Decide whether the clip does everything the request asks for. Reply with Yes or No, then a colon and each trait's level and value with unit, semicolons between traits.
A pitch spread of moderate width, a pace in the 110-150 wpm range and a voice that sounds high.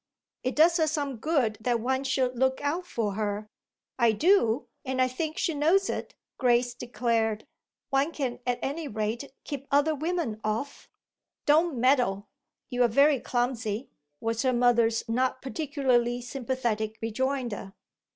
Yes: average, 3.8 semitones; average, 140 wpm; very high, 255 Hz